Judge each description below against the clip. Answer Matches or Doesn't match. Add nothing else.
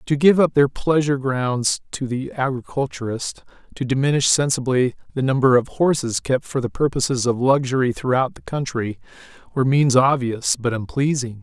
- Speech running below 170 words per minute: Matches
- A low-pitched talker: Matches